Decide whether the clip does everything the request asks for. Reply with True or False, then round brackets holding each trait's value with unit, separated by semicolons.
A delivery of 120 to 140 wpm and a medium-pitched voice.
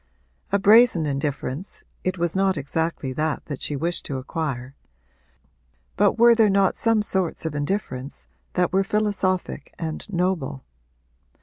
True (135 wpm; 170 Hz)